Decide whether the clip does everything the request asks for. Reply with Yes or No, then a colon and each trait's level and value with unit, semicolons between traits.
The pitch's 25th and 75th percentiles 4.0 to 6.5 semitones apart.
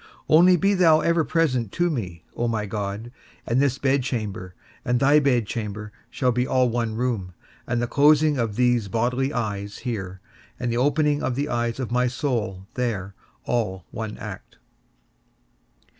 Yes: average, 4.4 semitones